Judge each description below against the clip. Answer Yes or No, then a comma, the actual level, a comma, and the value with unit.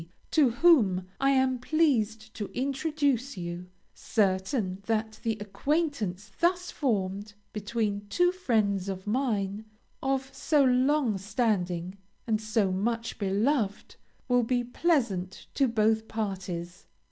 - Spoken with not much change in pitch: No, average, 5.1 semitones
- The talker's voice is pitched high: Yes, high, 220 Hz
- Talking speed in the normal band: No, slow, 115 wpm